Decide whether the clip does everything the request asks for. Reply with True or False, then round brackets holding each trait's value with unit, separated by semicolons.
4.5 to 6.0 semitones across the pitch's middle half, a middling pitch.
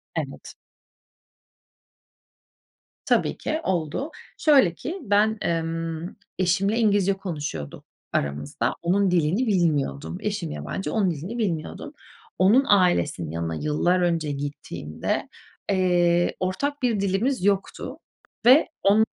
True (5.0 semitones; 180 Hz)